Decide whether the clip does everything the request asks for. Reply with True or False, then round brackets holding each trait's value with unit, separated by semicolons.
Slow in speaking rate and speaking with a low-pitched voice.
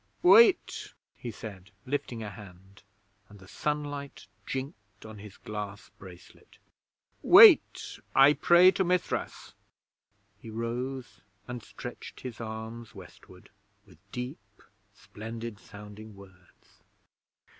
True (105 wpm; 110 Hz)